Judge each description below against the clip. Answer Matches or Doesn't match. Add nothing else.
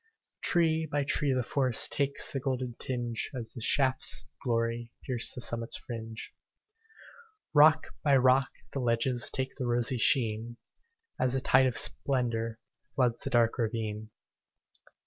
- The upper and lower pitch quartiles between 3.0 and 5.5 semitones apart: Doesn't match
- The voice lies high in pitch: Doesn't match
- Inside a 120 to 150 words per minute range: Matches